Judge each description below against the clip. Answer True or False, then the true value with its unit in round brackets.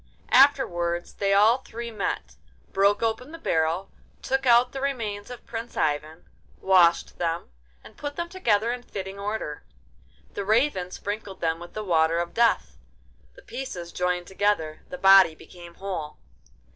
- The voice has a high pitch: True (200 Hz)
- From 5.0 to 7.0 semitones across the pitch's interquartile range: True (5.3 semitones)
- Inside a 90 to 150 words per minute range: True (145 wpm)